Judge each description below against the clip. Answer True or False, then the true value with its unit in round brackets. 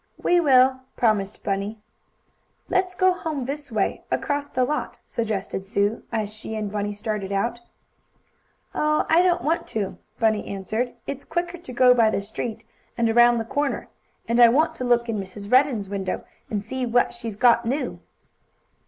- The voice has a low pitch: False (235 Hz)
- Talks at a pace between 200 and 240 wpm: False (170 wpm)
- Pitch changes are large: False (4.6 semitones)